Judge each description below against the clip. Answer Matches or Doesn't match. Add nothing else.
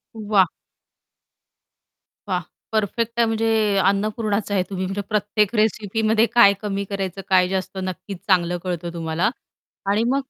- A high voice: Matches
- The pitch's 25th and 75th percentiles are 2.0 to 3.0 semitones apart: Matches